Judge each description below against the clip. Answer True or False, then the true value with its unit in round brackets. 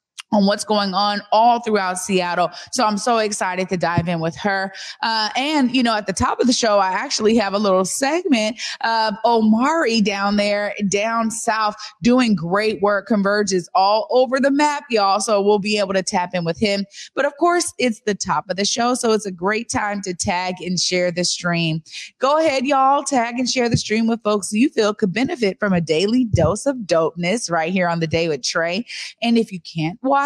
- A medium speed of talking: False (215 wpm)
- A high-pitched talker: True (210 Hz)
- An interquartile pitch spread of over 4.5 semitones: False (4.0 semitones)